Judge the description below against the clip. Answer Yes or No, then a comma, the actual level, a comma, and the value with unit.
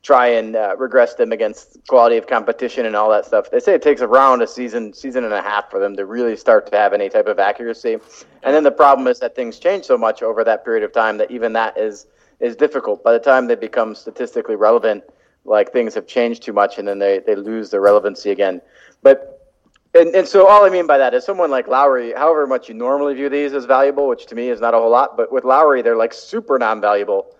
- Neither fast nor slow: No, fast, 245 wpm